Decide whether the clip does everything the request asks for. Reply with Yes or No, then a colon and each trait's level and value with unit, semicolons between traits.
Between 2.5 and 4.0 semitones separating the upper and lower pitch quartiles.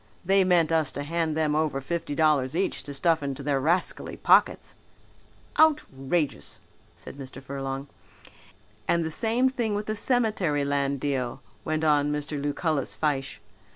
Yes: average, 3.5 semitones